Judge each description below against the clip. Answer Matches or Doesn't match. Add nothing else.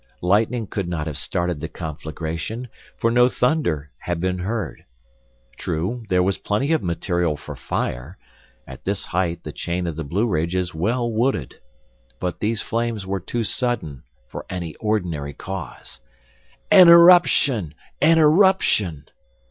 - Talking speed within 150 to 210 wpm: Doesn't match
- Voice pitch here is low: Matches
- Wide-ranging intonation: Matches